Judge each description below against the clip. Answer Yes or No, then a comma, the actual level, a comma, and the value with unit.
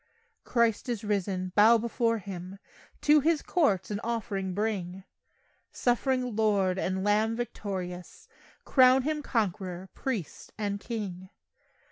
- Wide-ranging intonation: No, average, 3.8 semitones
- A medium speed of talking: No, slow, 115 wpm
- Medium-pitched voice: No, high, 210 Hz